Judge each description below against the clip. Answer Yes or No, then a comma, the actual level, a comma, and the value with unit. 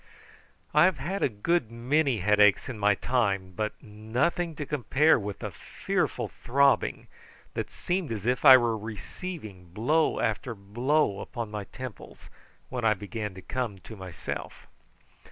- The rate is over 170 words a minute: No, average, 150 wpm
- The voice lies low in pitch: Yes, low, 115 Hz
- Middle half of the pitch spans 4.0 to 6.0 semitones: Yes, average, 5.2 semitones